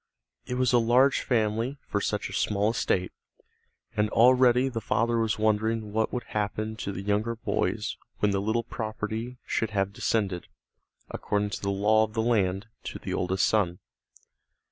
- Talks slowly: No, average, 165 wpm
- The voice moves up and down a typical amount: No, narrow, 2.2 semitones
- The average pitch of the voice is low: Yes, low, 110 Hz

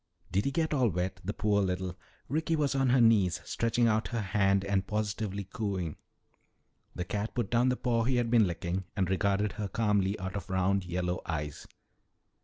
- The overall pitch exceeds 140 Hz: No, low, 100 Hz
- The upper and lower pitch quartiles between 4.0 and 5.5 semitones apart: No, average, 3.6 semitones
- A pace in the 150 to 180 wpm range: No, average, 195 wpm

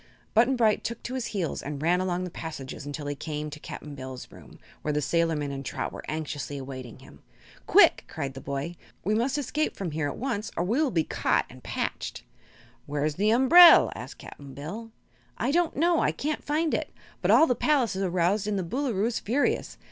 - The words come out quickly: Yes, fast, 210 wpm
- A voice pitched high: No, medium, 180 Hz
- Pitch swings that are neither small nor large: No, wide, 8.6 semitones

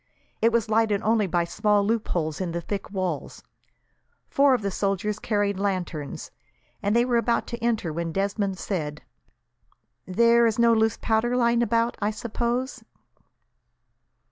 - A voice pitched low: No, high, 210 Hz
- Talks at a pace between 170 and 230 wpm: No, average, 145 wpm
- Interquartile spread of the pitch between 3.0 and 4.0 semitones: Yes, average, 3.6 semitones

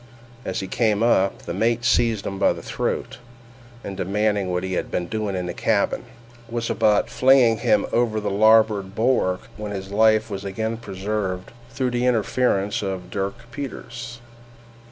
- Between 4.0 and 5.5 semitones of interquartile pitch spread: No, average, 3.1 semitones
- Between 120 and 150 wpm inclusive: No, average, 165 wpm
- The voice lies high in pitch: No, low, 105 Hz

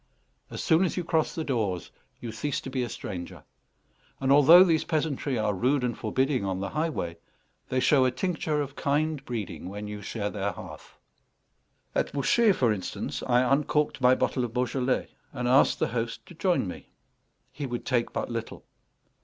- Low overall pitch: Yes, low, 130 Hz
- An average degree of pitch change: Yes, average, 4.6 semitones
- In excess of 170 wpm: Yes, average, 180 wpm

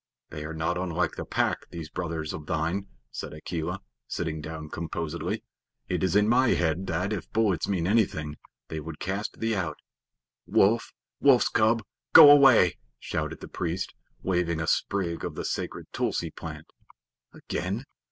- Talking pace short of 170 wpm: Yes, average, 155 wpm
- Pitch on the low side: Yes, very low, 90 Hz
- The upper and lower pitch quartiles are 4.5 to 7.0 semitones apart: No, average, 4.1 semitones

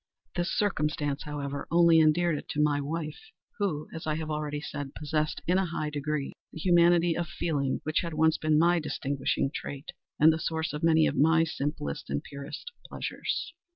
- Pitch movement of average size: No, narrow, 2.2 semitones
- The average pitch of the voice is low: No, medium, 155 Hz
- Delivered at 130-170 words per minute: No, average, 185 wpm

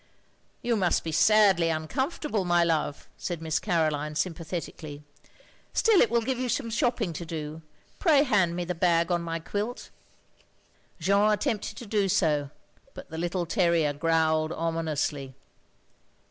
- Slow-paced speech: No, average, 145 wpm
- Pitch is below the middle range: No, medium, 170 Hz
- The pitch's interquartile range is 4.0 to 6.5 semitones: Yes, average, 4.8 semitones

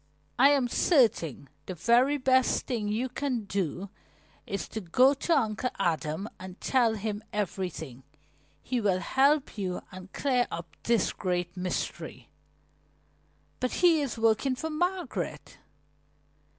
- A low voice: No, high, 220 Hz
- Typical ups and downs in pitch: No, wide, 6.0 semitones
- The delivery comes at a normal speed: No, slow, 130 wpm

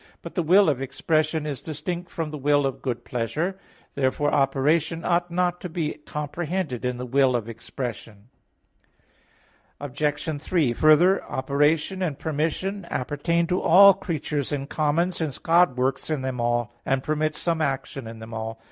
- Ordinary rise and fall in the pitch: Yes, average, 4.2 semitones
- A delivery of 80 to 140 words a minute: No, average, 165 wpm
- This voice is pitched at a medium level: Yes, medium, 150 Hz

